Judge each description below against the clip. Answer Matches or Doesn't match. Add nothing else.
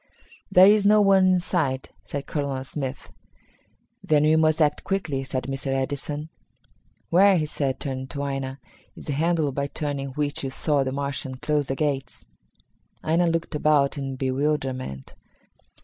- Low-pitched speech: Doesn't match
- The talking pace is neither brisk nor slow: Matches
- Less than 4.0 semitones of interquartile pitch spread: Matches